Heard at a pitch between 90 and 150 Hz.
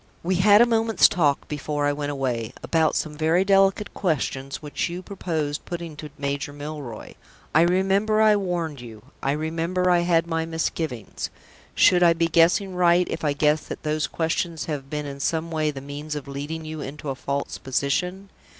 No: medium, 160 Hz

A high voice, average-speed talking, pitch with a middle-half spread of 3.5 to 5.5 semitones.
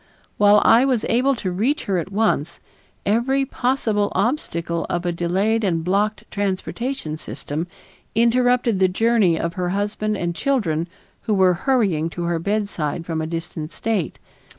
Yes: high, 200 Hz; average, 150 wpm; average, 5.0 semitones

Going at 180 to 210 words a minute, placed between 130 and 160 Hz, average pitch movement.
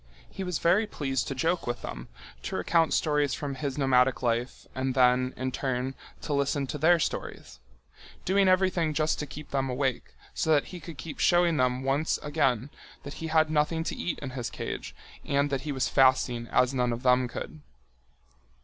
Yes: average, 185 wpm; medium, 140 Hz; average, 3.5 semitones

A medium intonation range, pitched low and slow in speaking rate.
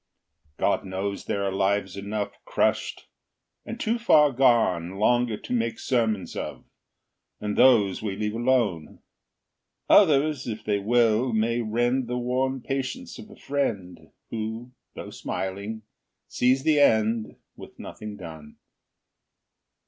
Yes: average, 4.2 semitones; low, 115 Hz; slow, 125 wpm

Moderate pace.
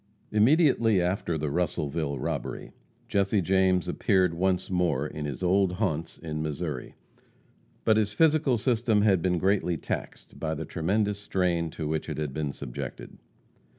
Yes: average, 150 wpm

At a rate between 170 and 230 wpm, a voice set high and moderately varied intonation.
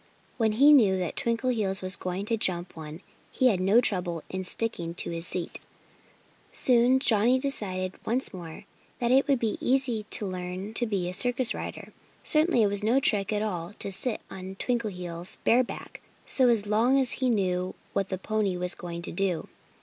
Yes: average, 185 wpm; high, 205 Hz; average, 4.7 semitones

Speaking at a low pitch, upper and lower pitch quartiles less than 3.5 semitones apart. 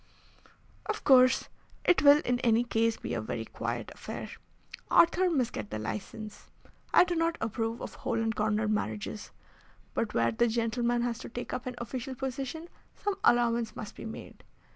No: high, 235 Hz; average, 2.9 semitones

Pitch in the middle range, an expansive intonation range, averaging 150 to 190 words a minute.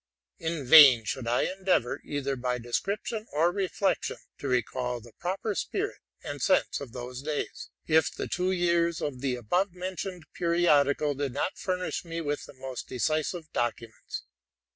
Yes: medium, 150 Hz; wide, 5.8 semitones; average, 155 wpm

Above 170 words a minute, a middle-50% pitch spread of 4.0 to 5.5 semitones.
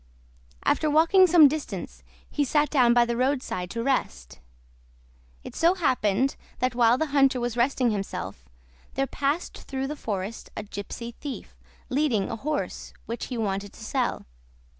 No: average, 155 wpm; average, 4.4 semitones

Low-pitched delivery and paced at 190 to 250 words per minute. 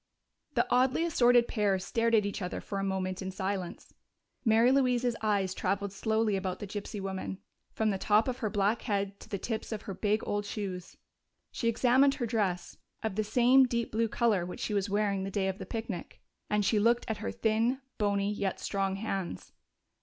No: high, 210 Hz; average, 200 wpm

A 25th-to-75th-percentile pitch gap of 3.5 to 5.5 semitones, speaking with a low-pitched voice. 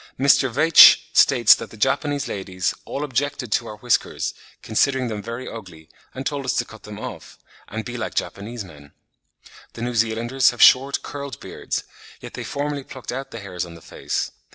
Yes: average, 4.2 semitones; low, 120 Hz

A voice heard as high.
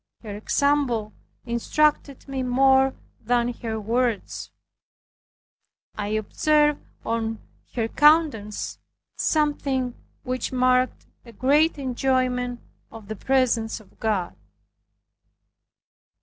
Yes: very high, 250 Hz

